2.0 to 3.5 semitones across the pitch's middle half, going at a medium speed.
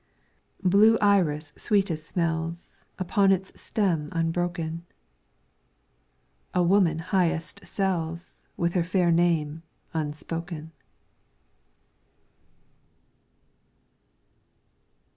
No: narrow, 2.5 semitones; slow, 70 wpm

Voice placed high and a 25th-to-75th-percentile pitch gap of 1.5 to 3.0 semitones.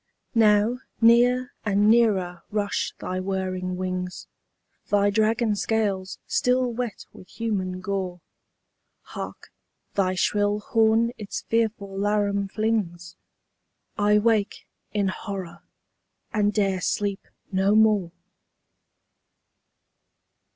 Yes: high, 205 Hz; average, 2.7 semitones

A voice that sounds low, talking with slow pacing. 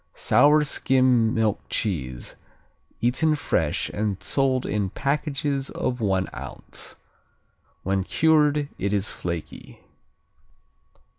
Yes: low, 120 Hz; slow, 95 wpm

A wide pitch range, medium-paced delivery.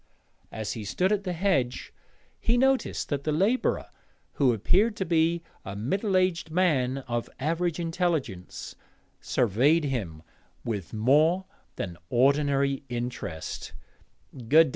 No: wide, 6.9 semitones; slow, 120 wpm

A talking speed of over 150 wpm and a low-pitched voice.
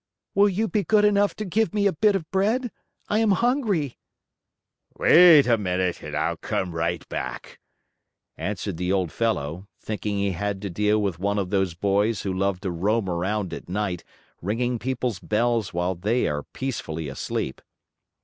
Yes: average, 170 wpm; low, 105 Hz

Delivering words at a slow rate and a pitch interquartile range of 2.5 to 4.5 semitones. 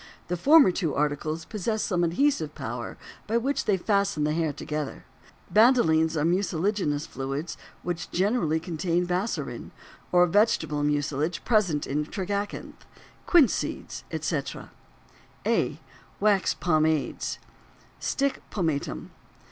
No: slow, 115 wpm; average, 5.2 semitones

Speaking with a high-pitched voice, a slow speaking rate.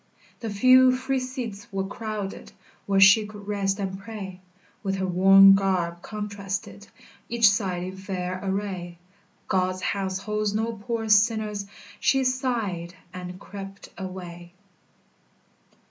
Yes: high, 200 Hz; slow, 125 wpm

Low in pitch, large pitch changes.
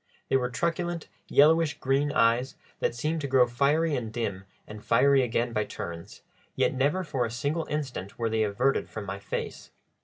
No: low, 130 Hz; average, 4.5 semitones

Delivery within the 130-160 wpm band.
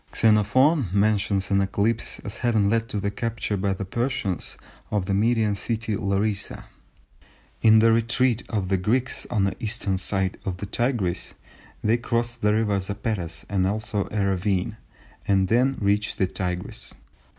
Yes: average, 155 wpm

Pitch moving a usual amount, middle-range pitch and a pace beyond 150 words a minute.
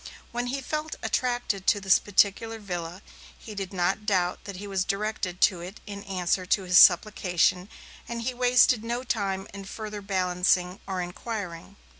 No: average, 3.4 semitones; high, 200 Hz; average, 165 wpm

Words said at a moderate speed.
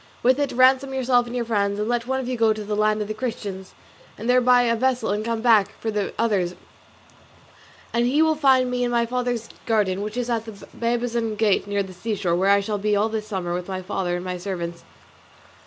No: fast, 235 wpm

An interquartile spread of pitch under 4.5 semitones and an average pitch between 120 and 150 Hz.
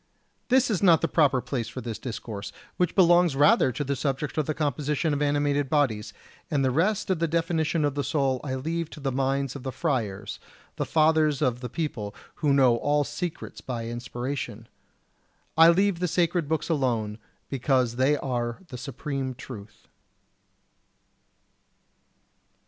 Yes: average, 4.1 semitones; medium, 140 Hz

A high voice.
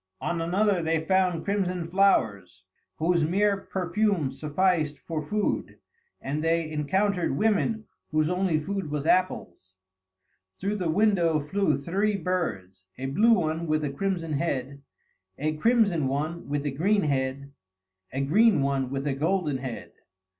No: medium, 165 Hz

